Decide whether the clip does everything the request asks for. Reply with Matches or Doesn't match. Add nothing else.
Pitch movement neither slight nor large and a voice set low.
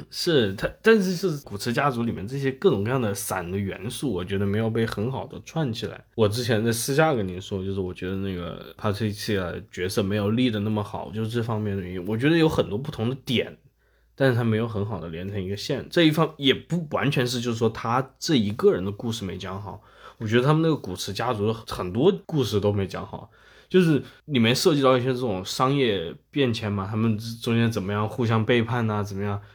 Matches